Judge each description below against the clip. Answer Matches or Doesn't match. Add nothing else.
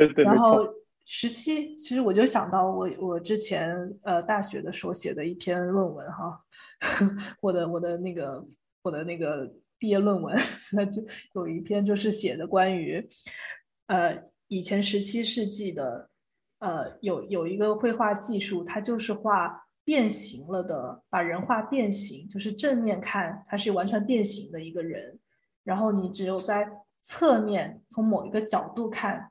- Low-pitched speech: Doesn't match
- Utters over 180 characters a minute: Matches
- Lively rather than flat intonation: Doesn't match